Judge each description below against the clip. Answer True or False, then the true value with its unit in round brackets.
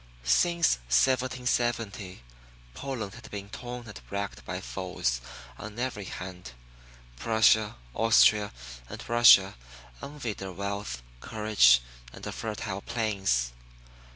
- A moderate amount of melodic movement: True (3.9 semitones)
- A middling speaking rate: False (105 wpm)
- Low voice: True (105 Hz)